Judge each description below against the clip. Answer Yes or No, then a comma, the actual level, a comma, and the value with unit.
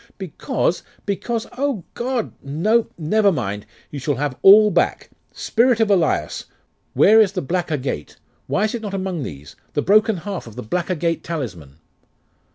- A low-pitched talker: No, medium, 180 Hz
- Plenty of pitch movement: Yes, wide, 7.2 semitones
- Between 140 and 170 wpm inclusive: Yes, average, 165 wpm